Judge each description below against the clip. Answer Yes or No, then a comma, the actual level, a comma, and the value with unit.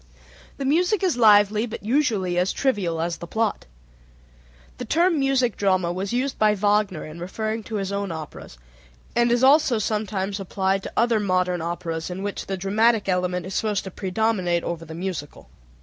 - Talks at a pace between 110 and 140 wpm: No, average, 175 wpm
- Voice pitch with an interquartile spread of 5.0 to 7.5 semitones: No, average, 4.0 semitones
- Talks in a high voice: Yes, high, 200 Hz